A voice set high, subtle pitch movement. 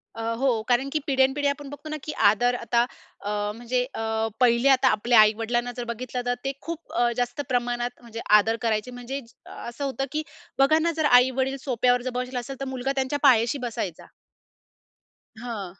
Yes: very high, 250 Hz; narrow, 2.3 semitones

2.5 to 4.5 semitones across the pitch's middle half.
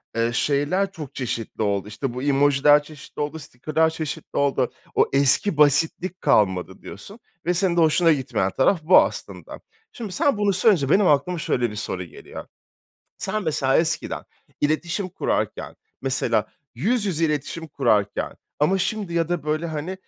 No: average, 5.0 semitones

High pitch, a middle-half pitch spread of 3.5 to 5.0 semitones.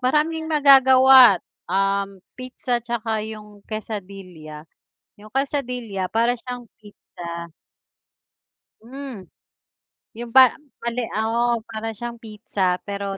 Yes: high, 225 Hz; average, 4.0 semitones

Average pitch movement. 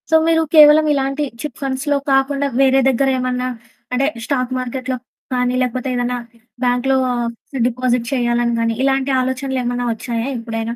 No: narrow, 1.8 semitones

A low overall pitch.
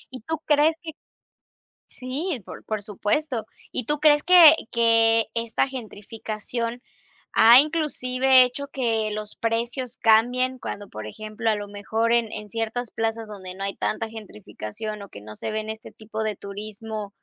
No: high, 225 Hz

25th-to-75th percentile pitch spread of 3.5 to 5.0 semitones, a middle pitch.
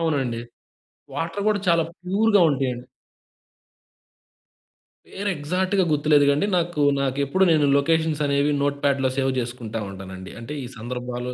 Yes: average, 4.7 semitones; medium, 145 Hz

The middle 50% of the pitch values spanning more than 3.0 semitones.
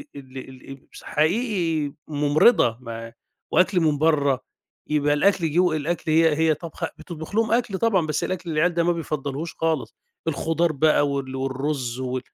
Yes: average, 3.4 semitones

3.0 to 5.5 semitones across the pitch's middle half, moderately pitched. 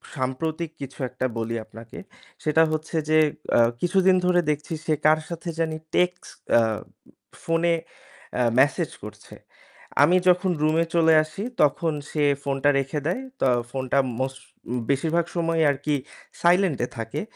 Yes: average, 3.8 semitones; medium, 155 Hz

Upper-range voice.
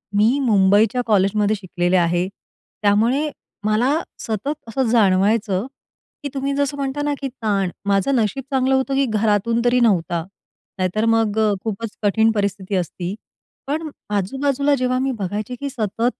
Yes: high, 220 Hz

